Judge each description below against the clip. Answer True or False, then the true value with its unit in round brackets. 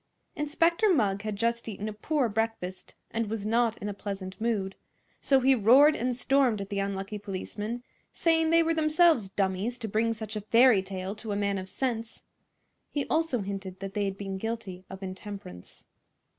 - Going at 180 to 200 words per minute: True (185 wpm)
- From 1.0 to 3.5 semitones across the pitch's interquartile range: False (4.0 semitones)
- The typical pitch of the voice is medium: False (215 Hz)